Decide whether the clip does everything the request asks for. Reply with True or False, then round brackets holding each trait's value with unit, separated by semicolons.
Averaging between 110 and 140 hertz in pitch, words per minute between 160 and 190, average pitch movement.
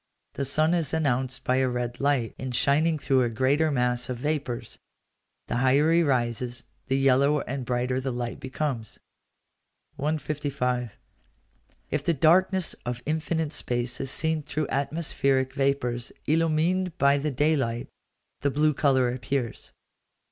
False (135 Hz; 140 wpm; 3.6 semitones)